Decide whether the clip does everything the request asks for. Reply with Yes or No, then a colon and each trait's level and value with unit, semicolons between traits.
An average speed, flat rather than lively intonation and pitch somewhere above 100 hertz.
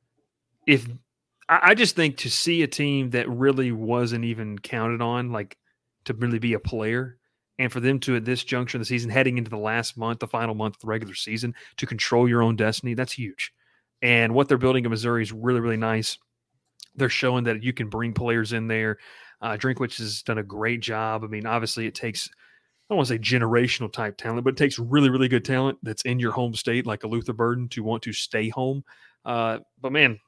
No: fast, 220 wpm; narrow, 2.1 semitones; low, 120 Hz